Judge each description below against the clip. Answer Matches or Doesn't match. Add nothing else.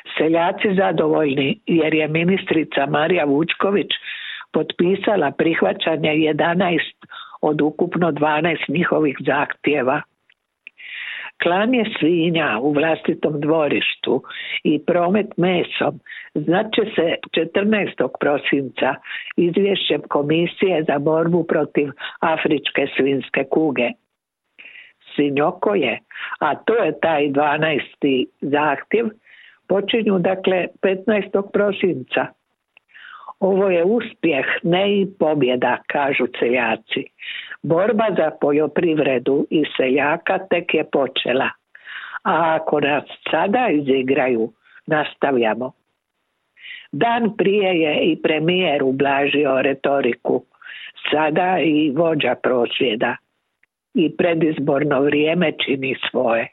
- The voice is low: Doesn't match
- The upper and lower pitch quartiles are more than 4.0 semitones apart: Matches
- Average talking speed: Doesn't match